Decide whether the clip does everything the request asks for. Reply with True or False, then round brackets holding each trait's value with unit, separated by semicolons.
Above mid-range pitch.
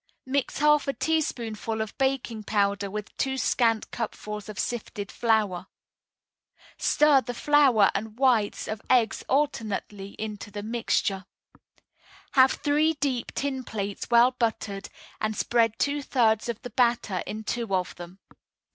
True (225 Hz)